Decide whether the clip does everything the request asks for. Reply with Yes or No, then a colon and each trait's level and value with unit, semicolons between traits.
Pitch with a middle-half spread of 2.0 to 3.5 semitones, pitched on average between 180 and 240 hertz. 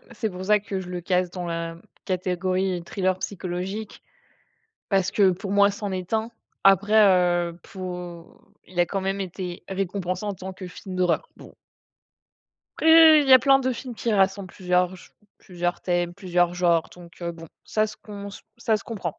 Yes: narrow, 2.4 semitones; medium, 185 Hz